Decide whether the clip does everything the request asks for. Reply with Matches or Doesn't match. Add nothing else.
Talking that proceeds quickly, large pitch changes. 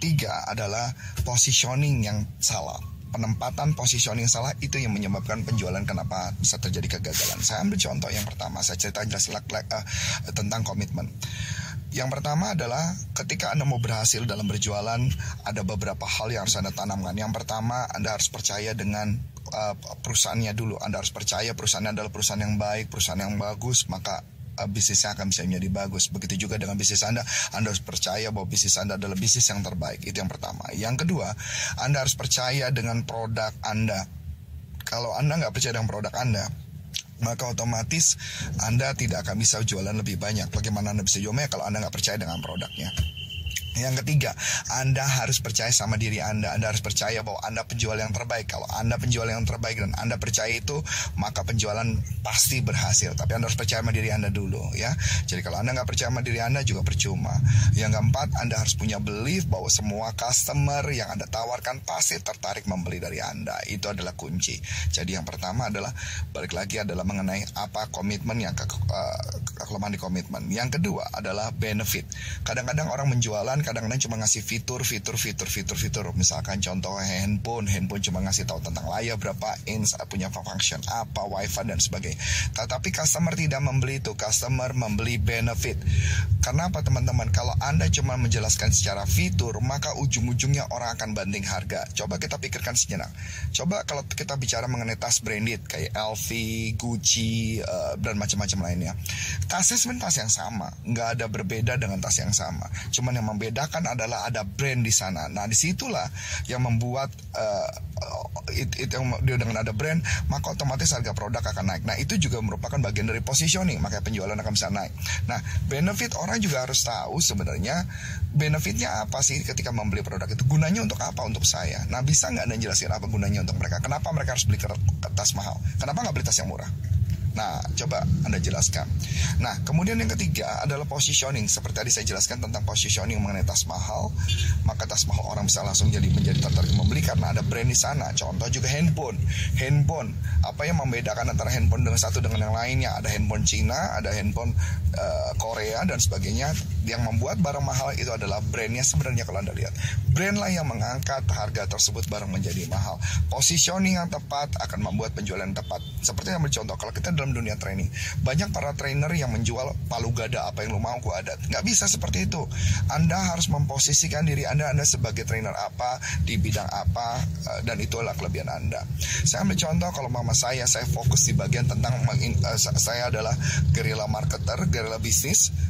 Doesn't match